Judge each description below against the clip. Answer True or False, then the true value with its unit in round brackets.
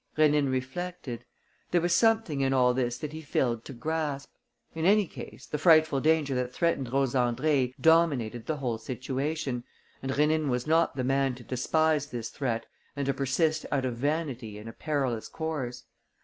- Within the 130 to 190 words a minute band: True (175 wpm)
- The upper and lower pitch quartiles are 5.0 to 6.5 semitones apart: False (3.9 semitones)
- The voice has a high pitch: False (140 Hz)